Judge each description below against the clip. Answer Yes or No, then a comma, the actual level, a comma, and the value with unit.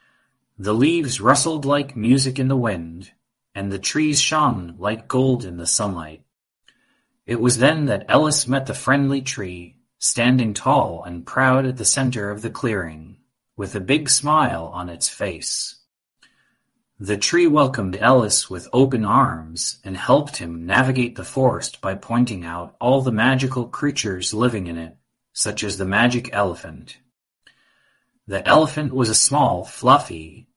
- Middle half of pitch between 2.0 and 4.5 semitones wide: No, wide, 5.4 semitones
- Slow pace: No, average, 150 wpm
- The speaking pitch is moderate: No, low, 120 Hz